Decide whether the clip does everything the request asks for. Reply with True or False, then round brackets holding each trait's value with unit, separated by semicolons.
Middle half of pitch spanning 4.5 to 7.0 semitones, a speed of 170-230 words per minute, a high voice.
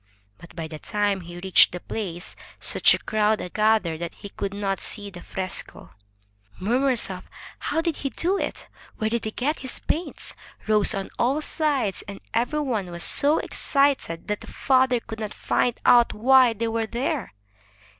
True (5.2 semitones; 180 wpm; 220 Hz)